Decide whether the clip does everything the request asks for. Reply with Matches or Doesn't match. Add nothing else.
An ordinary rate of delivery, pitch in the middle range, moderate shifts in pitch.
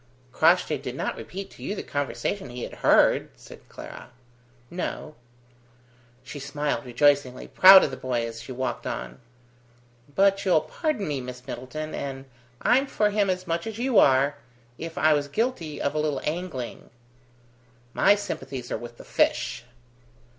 Doesn't match